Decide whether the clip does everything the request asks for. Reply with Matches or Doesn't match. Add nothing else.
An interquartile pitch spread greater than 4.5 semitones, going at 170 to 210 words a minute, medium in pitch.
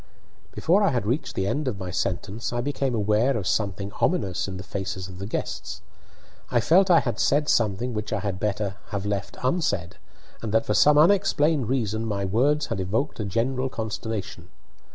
Doesn't match